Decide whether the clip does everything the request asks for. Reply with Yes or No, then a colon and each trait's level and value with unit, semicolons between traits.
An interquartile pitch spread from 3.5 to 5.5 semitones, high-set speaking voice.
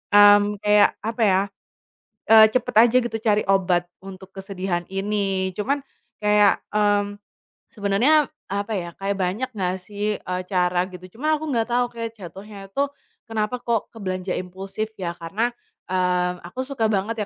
No: average, 3.0 semitones; high, 205 Hz